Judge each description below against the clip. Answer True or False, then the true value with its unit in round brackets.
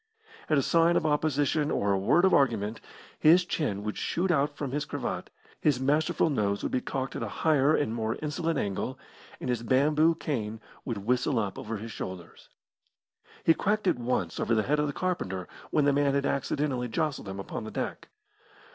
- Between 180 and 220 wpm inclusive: True (195 wpm)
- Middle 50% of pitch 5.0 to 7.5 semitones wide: True (5.5 semitones)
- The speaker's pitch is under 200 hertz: True (140 Hz)